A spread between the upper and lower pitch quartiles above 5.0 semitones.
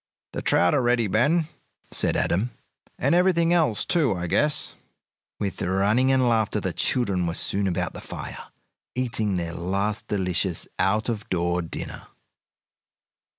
Yes: wide, 5.6 semitones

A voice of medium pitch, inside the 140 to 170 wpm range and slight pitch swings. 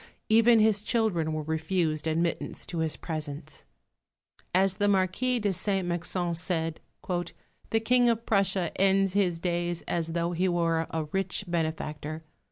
No: medium, 175 Hz; average, 145 wpm; average, 3.3 semitones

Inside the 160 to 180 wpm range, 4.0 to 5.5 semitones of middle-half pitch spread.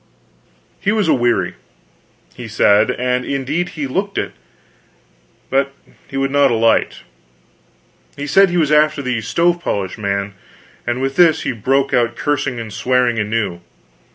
No: average, 145 wpm; average, 4.4 semitones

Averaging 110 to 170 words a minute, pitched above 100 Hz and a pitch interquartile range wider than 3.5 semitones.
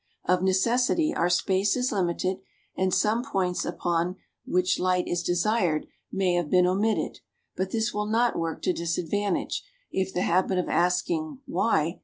No: average, 155 wpm; medium, 185 Hz; average, 3.2 semitones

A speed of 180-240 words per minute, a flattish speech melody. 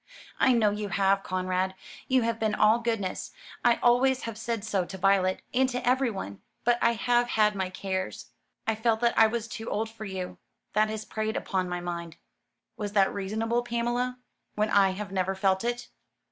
No: average, 190 wpm; average, 3.5 semitones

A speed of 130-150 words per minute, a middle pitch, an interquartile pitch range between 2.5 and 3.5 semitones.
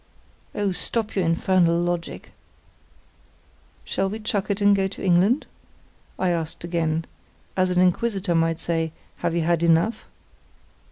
Yes: slow, 135 wpm; medium, 180 Hz; average, 2.8 semitones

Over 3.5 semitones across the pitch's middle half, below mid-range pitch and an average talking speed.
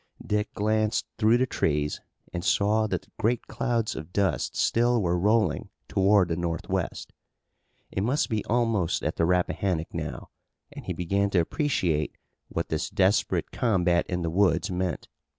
Yes: average, 3.9 semitones; low, 100 Hz; average, 150 wpm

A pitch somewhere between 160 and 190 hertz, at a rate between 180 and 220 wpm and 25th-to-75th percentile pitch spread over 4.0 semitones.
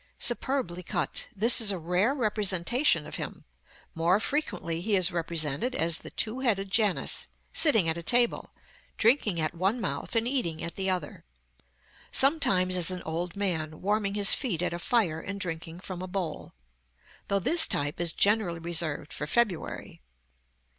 No: medium, 185 Hz; average, 165 wpm; average, 4.7 semitones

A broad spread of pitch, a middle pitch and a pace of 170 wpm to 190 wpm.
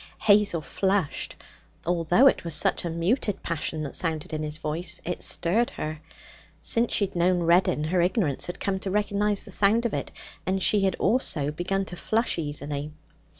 No: average, 4.3 semitones; medium, 180 Hz; average, 180 wpm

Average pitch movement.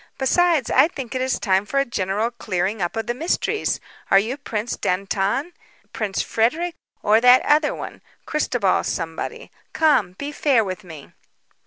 No: wide, 6.5 semitones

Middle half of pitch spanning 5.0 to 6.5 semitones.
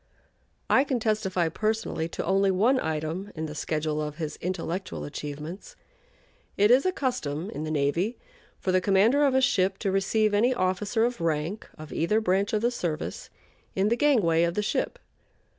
Yes: average, 5.3 semitones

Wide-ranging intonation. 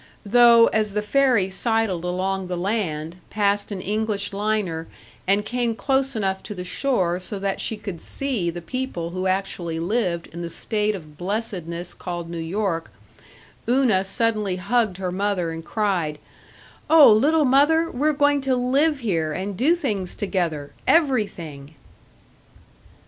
No: average, 5.0 semitones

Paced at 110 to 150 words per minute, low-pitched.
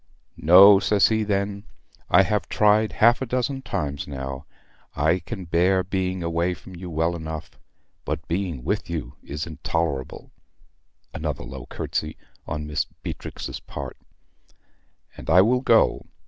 Yes: average, 140 wpm; very low, 90 Hz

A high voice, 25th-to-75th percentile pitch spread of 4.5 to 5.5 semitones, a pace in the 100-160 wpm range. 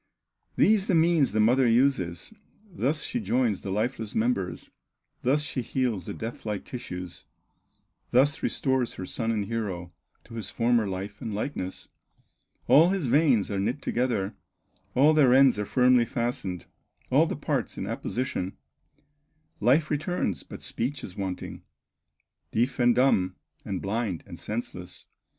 No: low, 120 Hz; average, 5.1 semitones; average, 145 wpm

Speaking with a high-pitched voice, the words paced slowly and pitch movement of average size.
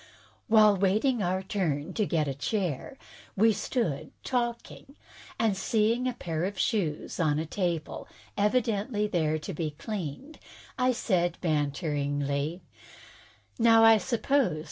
No: high, 195 Hz; slow, 130 wpm; wide, 6.3 semitones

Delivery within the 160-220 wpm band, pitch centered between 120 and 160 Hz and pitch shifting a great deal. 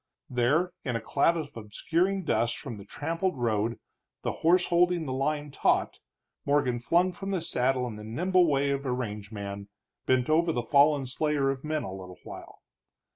Yes: average, 180 wpm; medium, 140 Hz; wide, 5.7 semitones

